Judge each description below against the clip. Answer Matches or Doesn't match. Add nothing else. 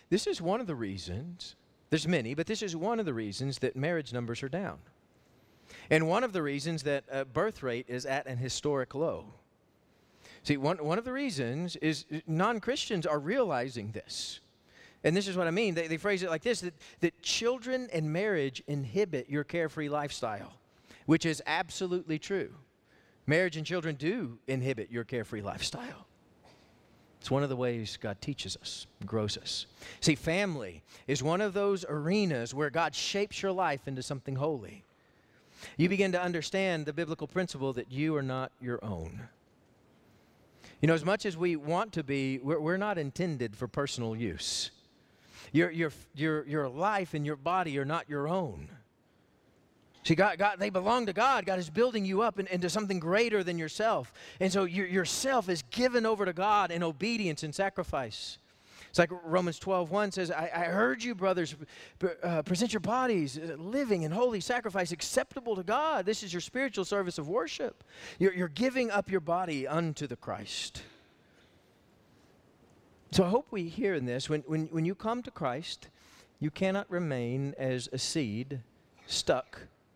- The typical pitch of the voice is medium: Matches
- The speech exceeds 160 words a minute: Matches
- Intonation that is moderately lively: Doesn't match